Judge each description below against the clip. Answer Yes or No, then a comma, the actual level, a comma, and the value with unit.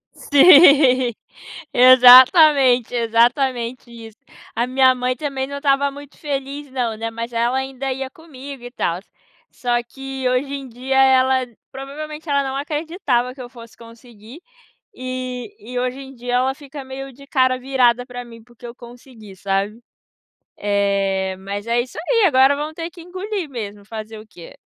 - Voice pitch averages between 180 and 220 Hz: No, very high, 255 Hz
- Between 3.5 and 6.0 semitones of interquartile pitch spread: No, average, 2.7 semitones